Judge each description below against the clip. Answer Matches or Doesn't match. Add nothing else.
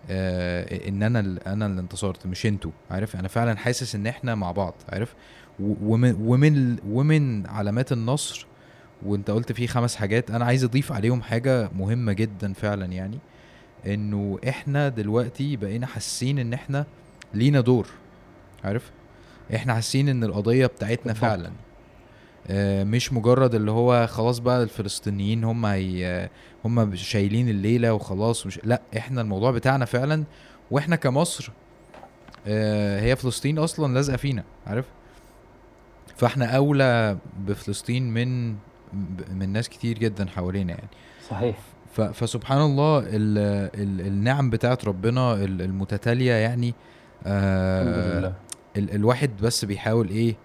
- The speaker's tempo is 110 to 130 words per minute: Matches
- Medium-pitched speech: Doesn't match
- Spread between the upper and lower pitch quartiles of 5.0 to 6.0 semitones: Doesn't match